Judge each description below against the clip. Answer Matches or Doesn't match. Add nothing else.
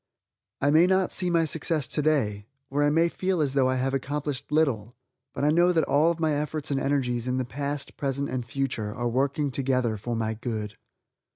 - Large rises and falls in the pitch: Doesn't match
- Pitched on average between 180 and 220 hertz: Doesn't match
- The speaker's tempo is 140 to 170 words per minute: Doesn't match